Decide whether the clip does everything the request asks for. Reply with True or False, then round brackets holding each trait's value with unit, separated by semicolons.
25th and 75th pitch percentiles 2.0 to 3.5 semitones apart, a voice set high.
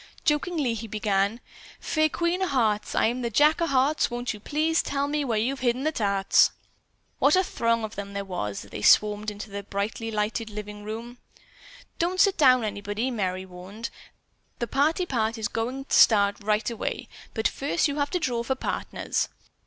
False (5.2 semitones; 230 Hz)